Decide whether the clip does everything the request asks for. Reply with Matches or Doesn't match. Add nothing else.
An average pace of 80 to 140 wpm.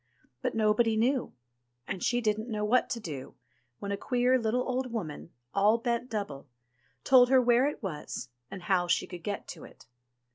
Doesn't match